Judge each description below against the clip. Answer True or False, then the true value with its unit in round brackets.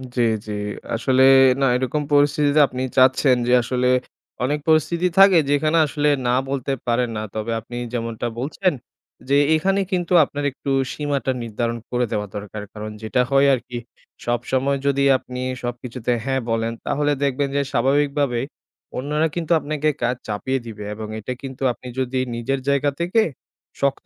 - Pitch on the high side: False (135 Hz)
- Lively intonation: False (3.2 semitones)